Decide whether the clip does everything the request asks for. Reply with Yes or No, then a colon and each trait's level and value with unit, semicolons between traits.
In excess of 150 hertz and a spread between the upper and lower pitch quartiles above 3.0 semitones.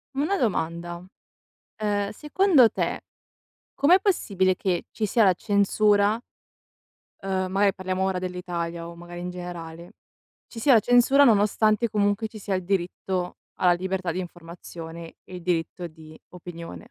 Yes: medium, 185 Hz; average, 3.5 semitones